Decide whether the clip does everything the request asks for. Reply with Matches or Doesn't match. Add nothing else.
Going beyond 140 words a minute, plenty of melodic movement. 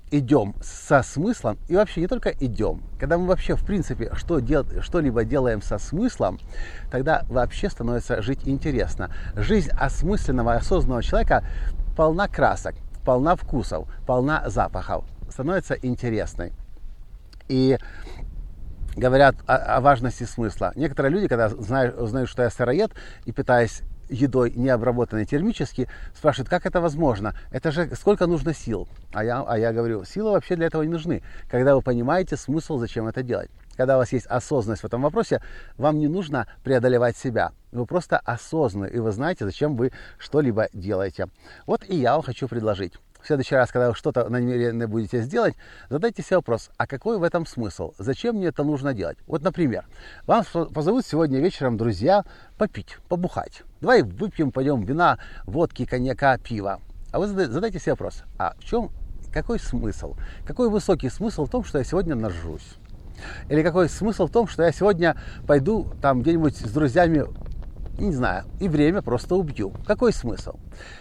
Matches